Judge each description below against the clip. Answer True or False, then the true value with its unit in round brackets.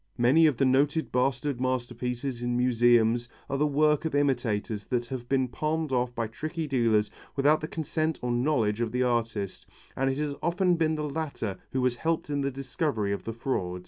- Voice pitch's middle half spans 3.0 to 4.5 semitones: True (3.9 semitones)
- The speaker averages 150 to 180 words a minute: False (195 wpm)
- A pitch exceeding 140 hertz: False (130 Hz)